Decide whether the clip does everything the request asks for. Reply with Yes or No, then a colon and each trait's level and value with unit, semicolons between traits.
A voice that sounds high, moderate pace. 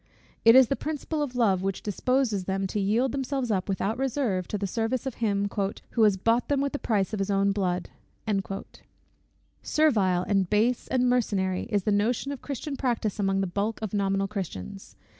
Yes: high, 210 Hz; average, 190 wpm